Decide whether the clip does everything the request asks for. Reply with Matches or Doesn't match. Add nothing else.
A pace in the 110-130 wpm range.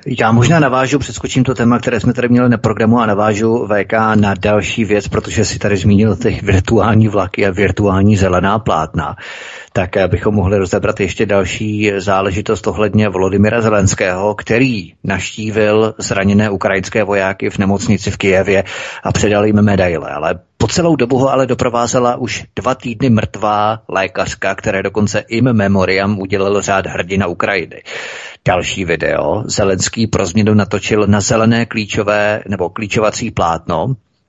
Doesn't match